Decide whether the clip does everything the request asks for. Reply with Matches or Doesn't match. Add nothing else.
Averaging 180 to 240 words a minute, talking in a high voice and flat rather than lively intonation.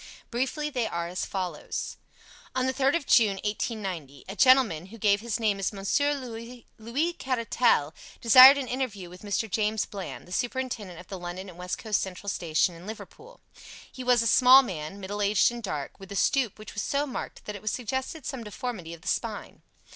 Doesn't match